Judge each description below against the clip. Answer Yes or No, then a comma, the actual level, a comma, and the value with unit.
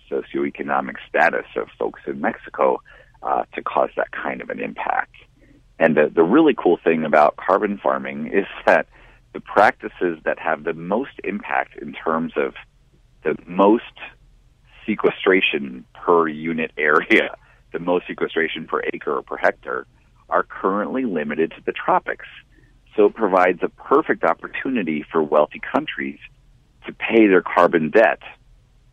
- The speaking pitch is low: Yes, very low, 80 Hz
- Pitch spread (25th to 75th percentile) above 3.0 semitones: No, narrow, 2.5 semitones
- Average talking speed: Yes, average, 145 wpm